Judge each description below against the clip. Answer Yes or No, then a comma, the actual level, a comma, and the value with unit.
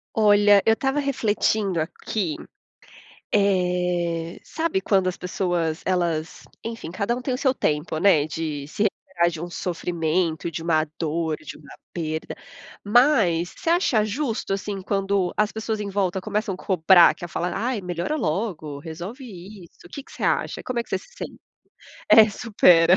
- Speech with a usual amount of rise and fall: Yes, average, 4.3 semitones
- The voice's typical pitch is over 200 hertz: No, medium, 185 Hz